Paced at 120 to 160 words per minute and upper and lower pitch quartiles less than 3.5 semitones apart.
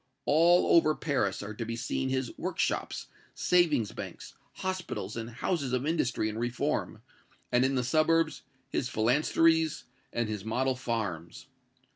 No: average, 140 wpm; wide, 5.4 semitones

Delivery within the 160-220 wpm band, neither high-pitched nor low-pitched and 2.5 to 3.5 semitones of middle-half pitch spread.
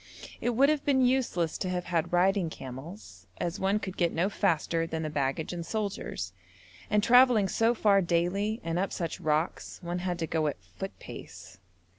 No: average, 185 wpm; medium, 180 Hz; average, 4.2 semitones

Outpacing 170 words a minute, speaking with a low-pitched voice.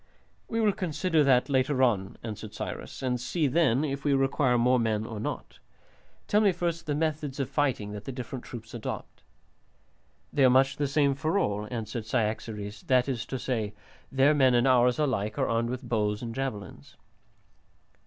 Yes: average, 180 wpm; low, 130 Hz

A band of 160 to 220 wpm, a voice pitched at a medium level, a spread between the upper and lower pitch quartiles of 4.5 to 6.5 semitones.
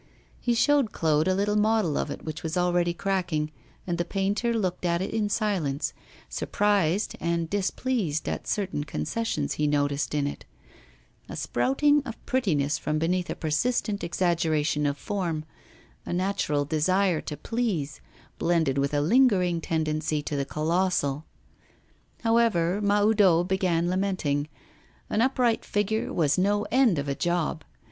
No: average, 145 wpm; medium, 175 Hz; average, 5.1 semitones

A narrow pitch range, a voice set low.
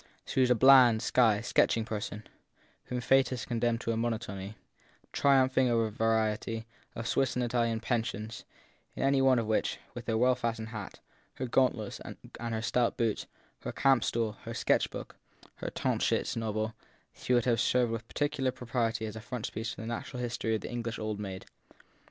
Yes: narrow, 2.0 semitones; low, 115 Hz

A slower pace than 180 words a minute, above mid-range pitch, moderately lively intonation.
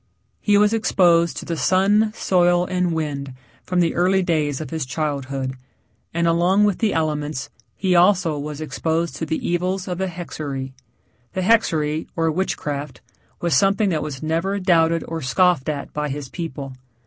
No: average, 165 wpm; medium, 165 Hz; average, 3.6 semitones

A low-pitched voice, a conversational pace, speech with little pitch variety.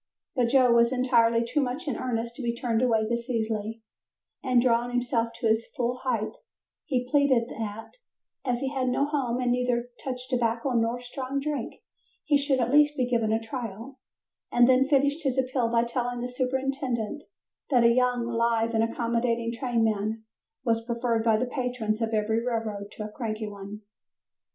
No: high, 240 Hz; average, 175 wpm; narrow, 2.0 semitones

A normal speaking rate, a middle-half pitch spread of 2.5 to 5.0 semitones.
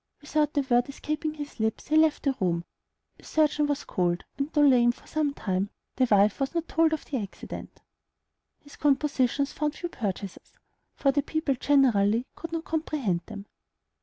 No: average, 175 wpm; wide, 5.4 semitones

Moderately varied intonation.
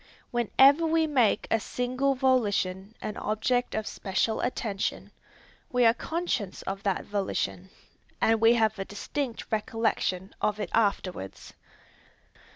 Yes: average, 3.9 semitones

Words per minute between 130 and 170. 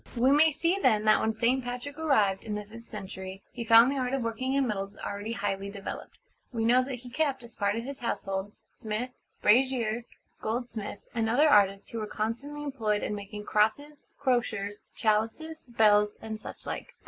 No: average, 185 wpm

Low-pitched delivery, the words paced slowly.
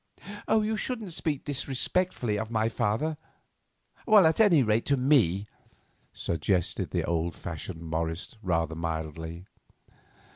Yes: low, 110 Hz; slow, 110 wpm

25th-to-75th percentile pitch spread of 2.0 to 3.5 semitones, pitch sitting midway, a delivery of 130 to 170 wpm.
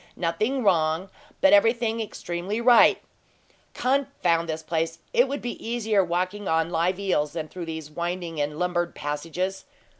No: average, 5.1 semitones; medium, 180 Hz; average, 145 wpm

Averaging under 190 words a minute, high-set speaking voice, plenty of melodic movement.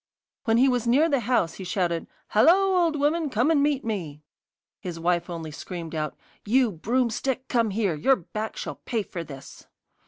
Yes: average, 180 wpm; high, 225 Hz; wide, 7.6 semitones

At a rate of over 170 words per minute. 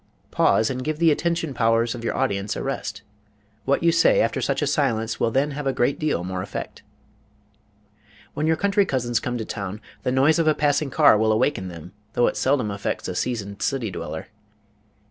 Yes: average, 200 wpm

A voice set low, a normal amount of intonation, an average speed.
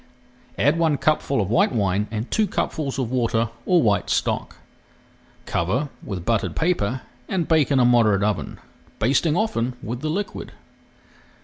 No: low, 125 Hz; wide, 6.3 semitones; average, 150 wpm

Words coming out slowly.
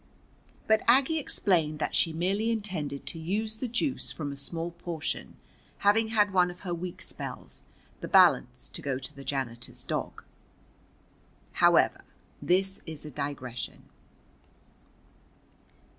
Yes: slow, 130 wpm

